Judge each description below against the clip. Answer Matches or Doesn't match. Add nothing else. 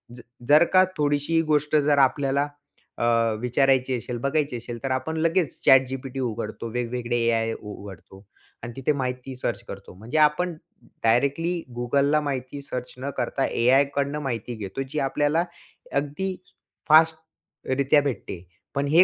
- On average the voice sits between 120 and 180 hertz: Matches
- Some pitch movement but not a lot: Matches